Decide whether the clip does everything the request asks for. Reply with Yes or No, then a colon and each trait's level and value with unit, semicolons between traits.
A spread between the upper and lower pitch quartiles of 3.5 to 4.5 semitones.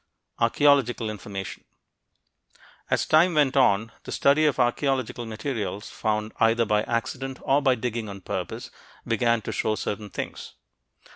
Yes: average, 3.9 semitones